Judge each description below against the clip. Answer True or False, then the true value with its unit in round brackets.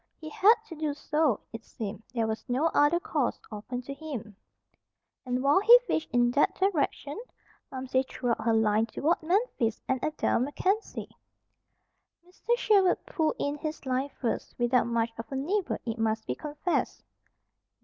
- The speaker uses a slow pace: False (160 wpm)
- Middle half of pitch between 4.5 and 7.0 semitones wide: True (5.3 semitones)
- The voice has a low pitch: False (275 Hz)